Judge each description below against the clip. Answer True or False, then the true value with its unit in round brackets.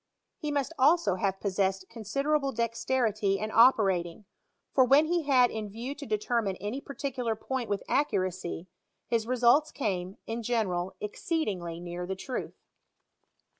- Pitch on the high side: True (225 Hz)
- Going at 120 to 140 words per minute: True (135 wpm)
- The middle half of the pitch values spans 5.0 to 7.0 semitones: True (5.5 semitones)